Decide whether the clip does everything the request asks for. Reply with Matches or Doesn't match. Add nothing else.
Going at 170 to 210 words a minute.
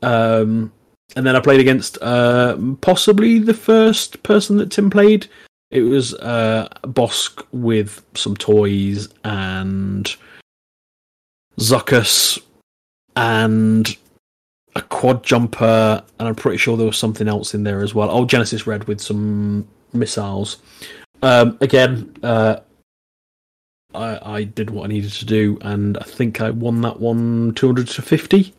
Doesn't match